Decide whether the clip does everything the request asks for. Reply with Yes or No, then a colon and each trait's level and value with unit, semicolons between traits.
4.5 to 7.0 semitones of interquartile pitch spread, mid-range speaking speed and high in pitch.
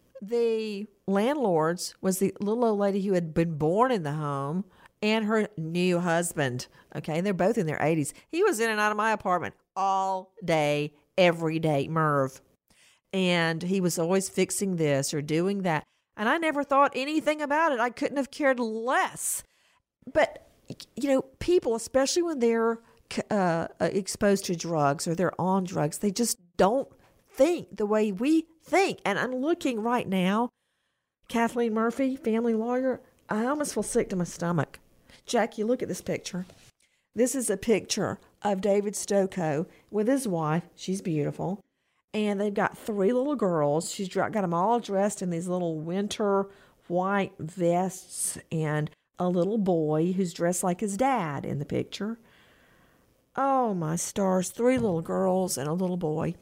Yes: average, 5.1 semitones; average, 165 wpm; high, 195 Hz